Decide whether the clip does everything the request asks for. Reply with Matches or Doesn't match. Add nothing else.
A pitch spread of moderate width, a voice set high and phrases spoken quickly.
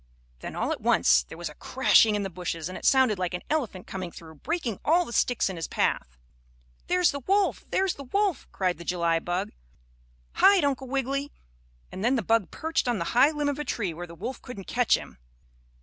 Doesn't match